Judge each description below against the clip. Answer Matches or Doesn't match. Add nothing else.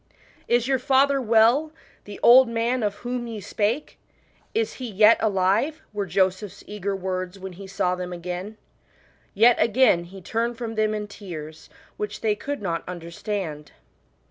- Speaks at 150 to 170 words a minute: Matches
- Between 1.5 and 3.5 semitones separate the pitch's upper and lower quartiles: Doesn't match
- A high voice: Matches